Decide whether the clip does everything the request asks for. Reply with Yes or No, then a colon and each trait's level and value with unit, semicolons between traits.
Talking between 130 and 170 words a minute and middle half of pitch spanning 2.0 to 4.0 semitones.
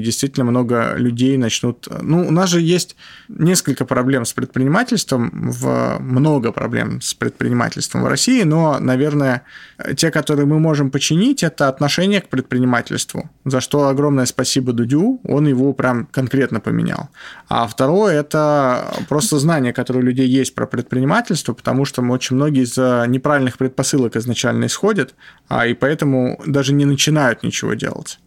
Yes: average, 145 wpm; average, 2.9 semitones